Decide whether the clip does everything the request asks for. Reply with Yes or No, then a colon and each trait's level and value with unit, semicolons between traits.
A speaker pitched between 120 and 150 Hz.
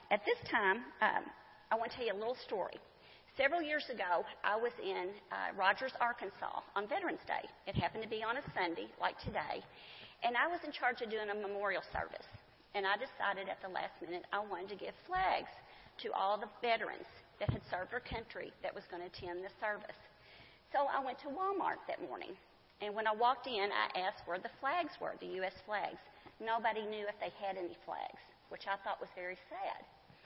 No: high, 220 Hz